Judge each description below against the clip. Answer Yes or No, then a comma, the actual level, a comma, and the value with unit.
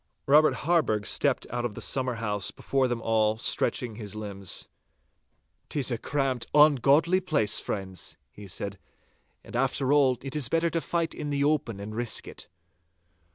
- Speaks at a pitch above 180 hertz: No, low, 125 Hz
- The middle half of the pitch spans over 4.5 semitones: Yes, average, 5.3 semitones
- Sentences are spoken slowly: No, average, 155 wpm